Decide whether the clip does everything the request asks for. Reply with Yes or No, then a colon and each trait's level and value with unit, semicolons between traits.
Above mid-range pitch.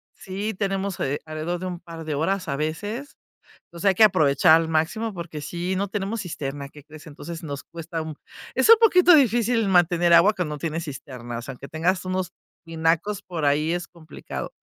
No: medium, 170 Hz